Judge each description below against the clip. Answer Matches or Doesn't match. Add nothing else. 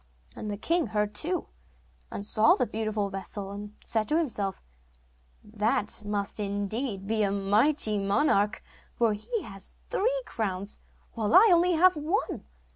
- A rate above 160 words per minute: Doesn't match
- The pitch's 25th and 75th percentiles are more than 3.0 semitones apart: Matches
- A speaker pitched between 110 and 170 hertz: Doesn't match